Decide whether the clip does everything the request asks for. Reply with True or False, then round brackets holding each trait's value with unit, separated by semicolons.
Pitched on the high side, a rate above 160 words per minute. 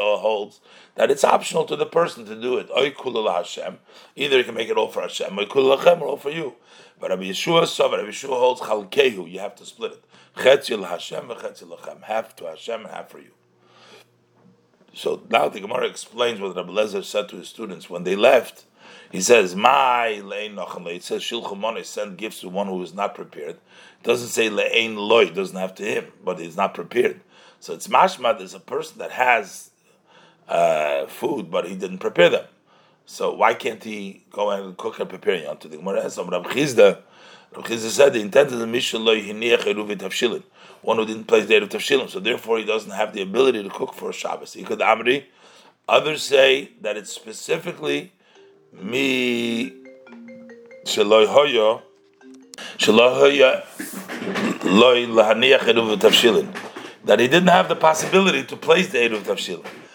False (255 Hz; 155 wpm)